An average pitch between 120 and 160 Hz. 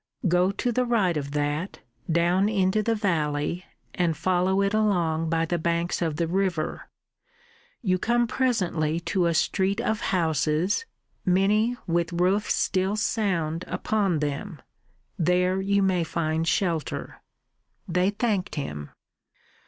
No: medium, 180 Hz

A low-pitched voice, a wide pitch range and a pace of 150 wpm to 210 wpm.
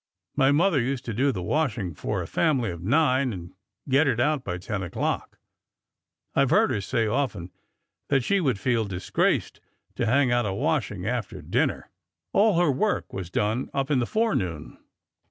Yes: low, 125 Hz; wide, 6.3 semitones; average, 180 wpm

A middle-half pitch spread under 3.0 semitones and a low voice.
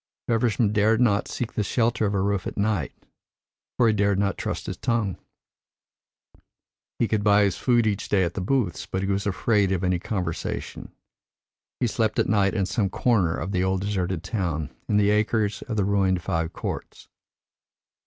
Yes: narrow, 2.6 semitones; low, 100 Hz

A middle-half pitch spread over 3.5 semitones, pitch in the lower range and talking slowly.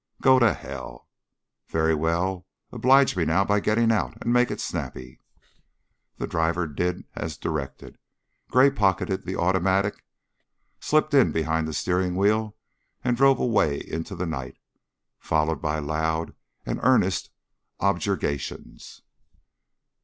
Yes: average, 5.1 semitones; very low, 90 Hz; slow, 125 wpm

